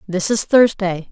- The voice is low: No, high, 200 Hz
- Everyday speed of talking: Yes, average, 160 wpm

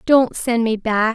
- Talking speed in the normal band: No, fast, 210 wpm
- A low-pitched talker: No, high, 230 Hz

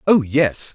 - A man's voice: Yes, male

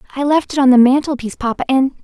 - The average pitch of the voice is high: Yes, very high, 265 Hz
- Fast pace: Yes, fast, 235 wpm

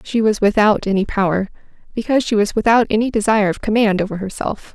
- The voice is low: No, high, 210 Hz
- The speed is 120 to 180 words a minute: No, average, 190 wpm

